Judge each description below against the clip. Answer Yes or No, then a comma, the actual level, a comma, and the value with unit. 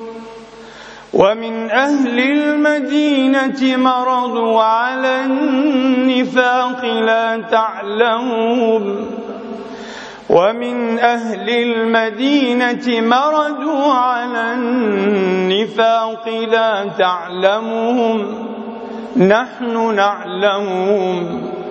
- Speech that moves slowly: Yes, slow, 50 wpm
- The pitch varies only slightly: Yes, narrow, 2.1 semitones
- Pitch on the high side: Yes, high, 230 Hz